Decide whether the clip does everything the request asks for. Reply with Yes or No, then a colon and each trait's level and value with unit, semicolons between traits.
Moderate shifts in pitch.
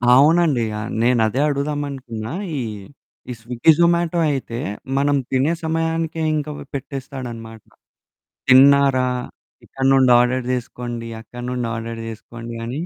Yes: average, 3.4 semitones